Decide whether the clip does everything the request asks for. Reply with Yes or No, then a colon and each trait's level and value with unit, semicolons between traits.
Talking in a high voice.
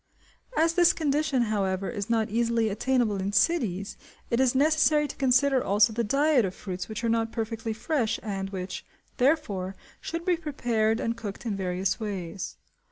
Yes: high, 225 Hz